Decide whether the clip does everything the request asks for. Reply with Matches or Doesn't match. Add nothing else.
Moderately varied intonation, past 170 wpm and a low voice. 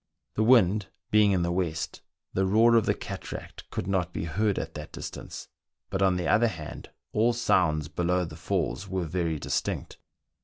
Matches